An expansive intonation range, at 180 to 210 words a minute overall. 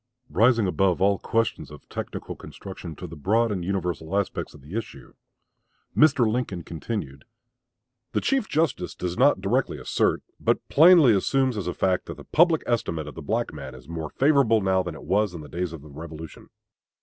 Yes: wide, 6.2 semitones; average, 185 wpm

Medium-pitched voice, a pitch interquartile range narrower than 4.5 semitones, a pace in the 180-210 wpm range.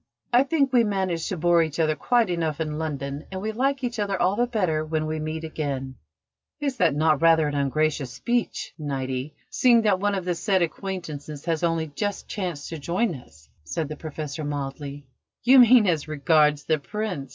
No: medium, 160 Hz; average, 5.3 semitones; average, 195 wpm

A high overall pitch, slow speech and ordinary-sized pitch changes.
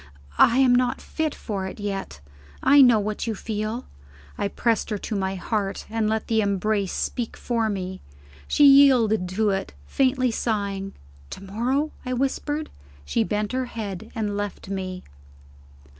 No: high, 215 Hz; average, 160 wpm; average, 3.9 semitones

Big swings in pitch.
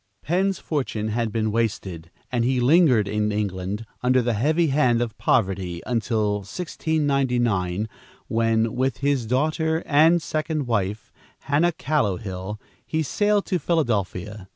Yes: wide, 6.2 semitones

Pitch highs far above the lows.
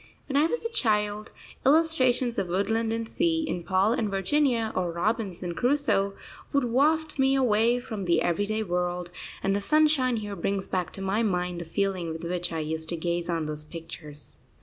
Yes: wide, 6.0 semitones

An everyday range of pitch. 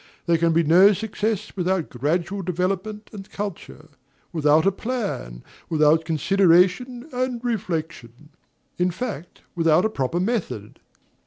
Yes: average, 4.6 semitones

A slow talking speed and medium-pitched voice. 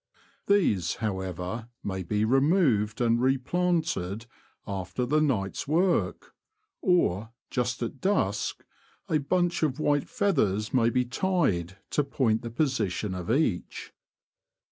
No: slow, 120 wpm; low, 120 Hz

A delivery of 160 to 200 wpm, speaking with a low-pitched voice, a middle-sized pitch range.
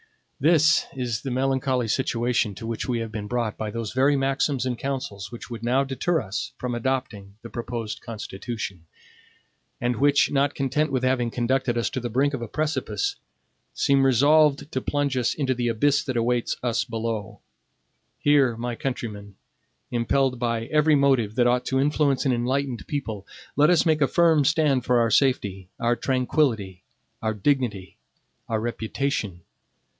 Yes: average, 165 wpm; low, 125 Hz; average, 3.2 semitones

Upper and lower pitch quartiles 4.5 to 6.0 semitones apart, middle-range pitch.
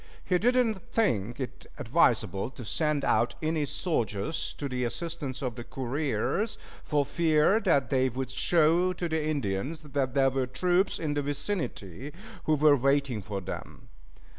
No: average, 4.1 semitones; medium, 145 Hz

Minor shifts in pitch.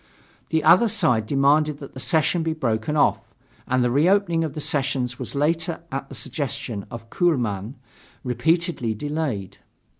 No: average, 4.7 semitones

